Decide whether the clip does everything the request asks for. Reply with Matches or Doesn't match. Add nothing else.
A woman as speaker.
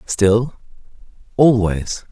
Doesn't match